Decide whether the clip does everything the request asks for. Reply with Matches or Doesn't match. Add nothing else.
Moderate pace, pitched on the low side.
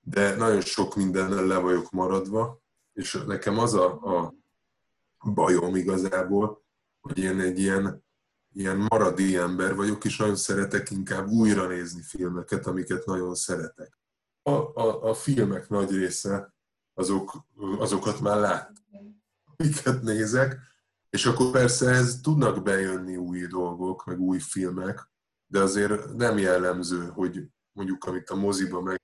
Matches